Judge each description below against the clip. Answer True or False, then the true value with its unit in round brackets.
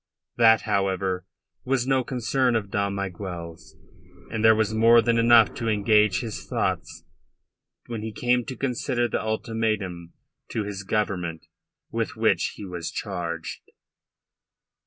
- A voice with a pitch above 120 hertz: False (110 Hz)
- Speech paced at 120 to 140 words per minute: True (135 wpm)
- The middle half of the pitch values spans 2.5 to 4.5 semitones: True (3.3 semitones)